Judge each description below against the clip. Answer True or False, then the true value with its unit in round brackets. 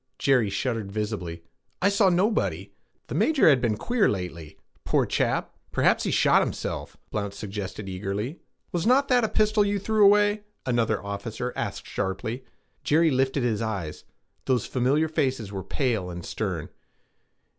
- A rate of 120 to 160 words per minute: True (150 wpm)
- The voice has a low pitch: True (120 Hz)